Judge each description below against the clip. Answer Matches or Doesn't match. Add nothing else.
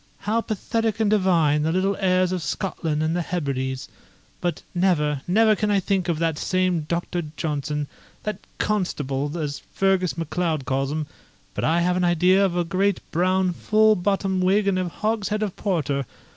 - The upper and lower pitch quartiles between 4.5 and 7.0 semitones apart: Doesn't match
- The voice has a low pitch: Doesn't match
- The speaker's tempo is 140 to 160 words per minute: Doesn't match